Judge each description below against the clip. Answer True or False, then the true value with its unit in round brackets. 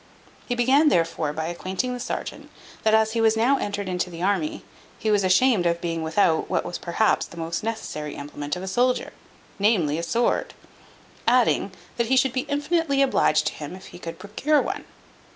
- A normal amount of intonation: False (6.4 semitones)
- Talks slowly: False (190 wpm)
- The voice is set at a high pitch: True (205 Hz)